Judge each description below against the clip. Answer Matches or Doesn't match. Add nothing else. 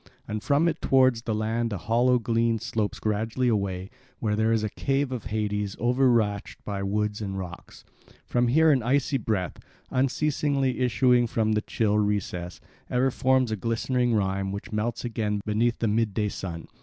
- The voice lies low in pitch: Matches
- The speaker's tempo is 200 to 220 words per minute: Doesn't match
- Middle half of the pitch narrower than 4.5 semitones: Matches